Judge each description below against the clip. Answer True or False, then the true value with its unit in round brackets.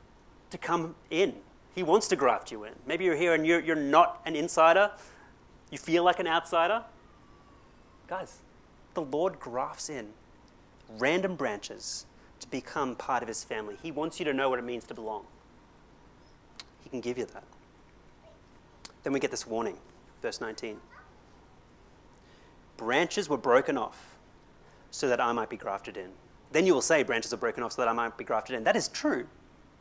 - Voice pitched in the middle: True (160 Hz)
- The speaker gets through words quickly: False (175 wpm)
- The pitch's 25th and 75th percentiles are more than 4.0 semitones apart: True (4.5 semitones)